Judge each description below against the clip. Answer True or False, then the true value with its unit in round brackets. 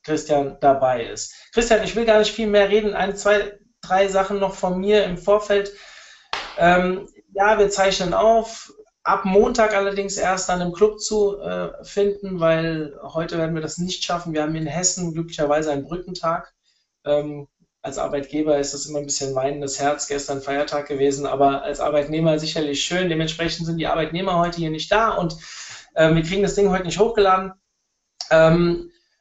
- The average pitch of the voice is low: False (175 Hz)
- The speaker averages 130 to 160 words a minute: False (175 wpm)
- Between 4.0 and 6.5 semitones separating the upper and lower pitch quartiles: True (4.7 semitones)